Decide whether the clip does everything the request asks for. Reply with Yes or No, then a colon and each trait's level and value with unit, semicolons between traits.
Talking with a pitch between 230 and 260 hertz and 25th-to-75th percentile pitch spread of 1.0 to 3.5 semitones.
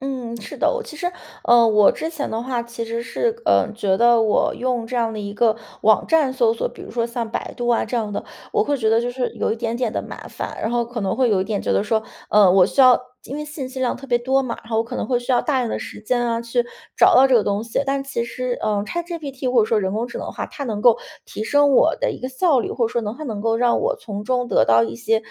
Yes: high, 235 Hz; average, 2.7 semitones